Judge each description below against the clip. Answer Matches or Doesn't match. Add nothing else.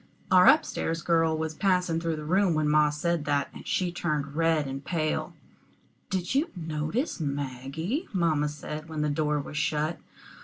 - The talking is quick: Doesn't match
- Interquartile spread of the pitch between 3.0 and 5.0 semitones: Doesn't match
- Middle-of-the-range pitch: Matches